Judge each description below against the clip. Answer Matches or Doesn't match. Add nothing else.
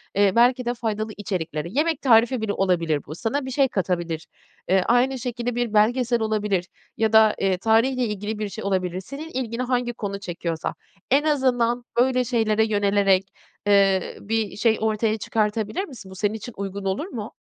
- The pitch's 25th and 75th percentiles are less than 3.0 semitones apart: Doesn't match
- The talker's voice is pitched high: Matches